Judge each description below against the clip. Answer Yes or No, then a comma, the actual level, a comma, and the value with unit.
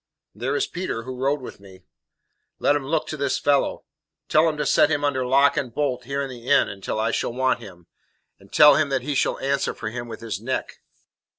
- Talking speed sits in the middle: No, fast, 225 wpm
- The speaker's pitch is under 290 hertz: Yes, low, 135 Hz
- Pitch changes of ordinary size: Yes, average, 3.4 semitones